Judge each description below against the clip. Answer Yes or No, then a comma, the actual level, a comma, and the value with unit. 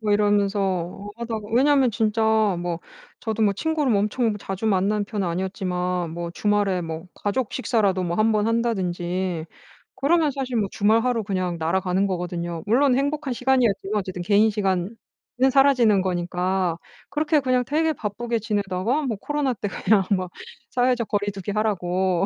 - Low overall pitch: No, high, 205 Hz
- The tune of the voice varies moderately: Yes, average, 4.3 semitones